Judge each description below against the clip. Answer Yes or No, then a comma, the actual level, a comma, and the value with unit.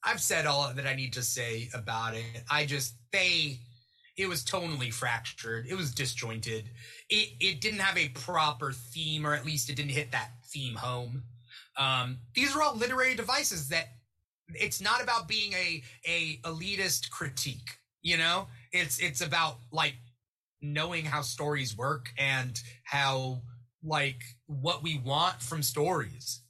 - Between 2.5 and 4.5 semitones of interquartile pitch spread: No, average, 5.1 semitones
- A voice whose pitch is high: No, medium, 140 Hz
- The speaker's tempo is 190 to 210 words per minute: No, average, 155 wpm